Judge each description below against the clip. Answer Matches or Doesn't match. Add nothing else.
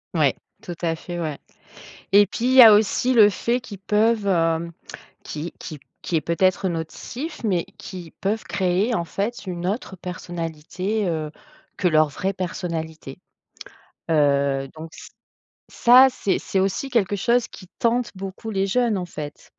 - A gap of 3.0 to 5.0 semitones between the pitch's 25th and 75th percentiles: Matches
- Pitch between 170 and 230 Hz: Matches